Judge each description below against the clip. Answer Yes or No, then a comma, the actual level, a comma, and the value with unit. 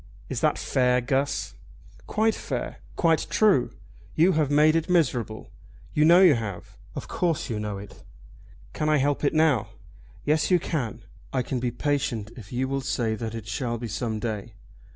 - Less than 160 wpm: No, average, 175 wpm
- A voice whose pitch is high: No, low, 130 Hz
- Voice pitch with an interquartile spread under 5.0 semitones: No, average, 5.3 semitones